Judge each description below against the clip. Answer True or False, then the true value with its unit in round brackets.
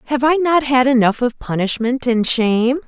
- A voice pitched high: True (250 Hz)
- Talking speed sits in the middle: True (190 wpm)